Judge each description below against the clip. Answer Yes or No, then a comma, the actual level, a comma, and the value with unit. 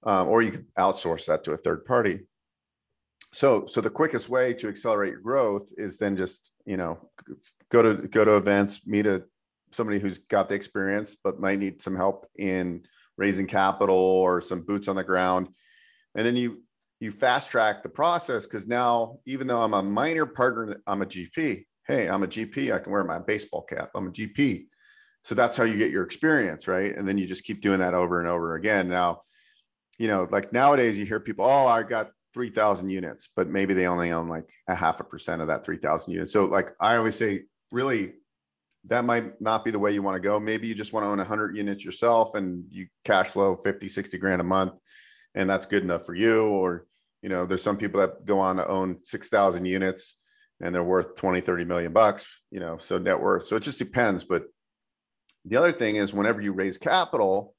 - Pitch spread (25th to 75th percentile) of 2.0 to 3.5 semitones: Yes, average, 2.9 semitones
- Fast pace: Yes, fast, 215 wpm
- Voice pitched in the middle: No, low, 100 Hz